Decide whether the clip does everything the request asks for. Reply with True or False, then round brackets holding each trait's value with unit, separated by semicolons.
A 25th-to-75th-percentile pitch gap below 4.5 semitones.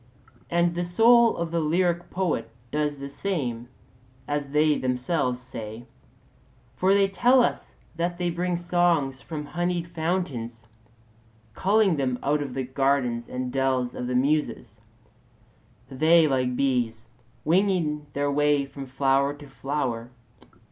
False (5.1 semitones)